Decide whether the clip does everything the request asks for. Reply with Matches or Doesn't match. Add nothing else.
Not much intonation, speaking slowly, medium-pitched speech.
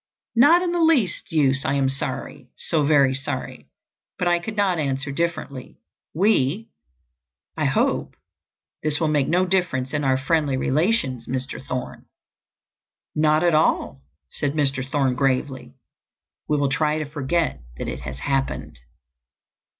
Doesn't match